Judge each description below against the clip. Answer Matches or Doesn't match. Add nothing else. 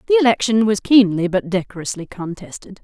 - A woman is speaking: Matches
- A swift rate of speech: Doesn't match